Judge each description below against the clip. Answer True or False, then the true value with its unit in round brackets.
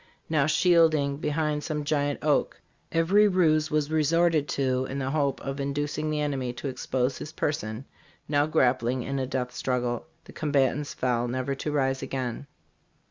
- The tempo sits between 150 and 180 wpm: True (165 wpm)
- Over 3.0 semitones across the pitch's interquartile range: False (2.7 semitones)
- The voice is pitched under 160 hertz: True (140 Hz)